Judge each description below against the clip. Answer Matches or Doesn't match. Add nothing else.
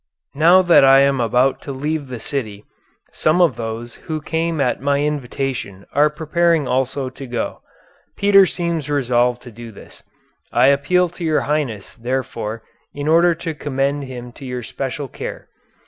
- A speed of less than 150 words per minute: Doesn't match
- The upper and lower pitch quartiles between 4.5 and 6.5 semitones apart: Doesn't match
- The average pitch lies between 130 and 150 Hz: Matches